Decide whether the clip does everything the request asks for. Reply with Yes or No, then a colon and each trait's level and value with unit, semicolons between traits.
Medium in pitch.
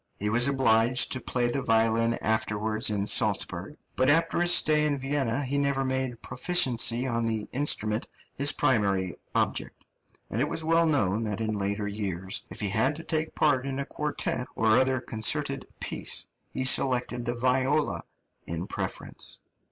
No: low, 125 Hz